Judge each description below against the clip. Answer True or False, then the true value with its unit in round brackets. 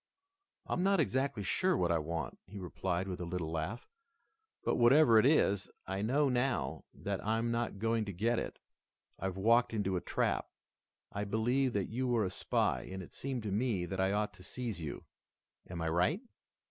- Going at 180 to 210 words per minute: True (190 wpm)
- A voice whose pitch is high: False (105 Hz)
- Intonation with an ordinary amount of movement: True (4.8 semitones)